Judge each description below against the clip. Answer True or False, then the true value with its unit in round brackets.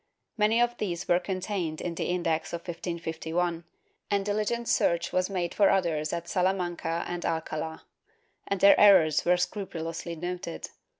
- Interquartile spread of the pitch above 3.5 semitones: False (2.8 semitones)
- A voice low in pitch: False (175 Hz)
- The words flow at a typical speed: True (145 wpm)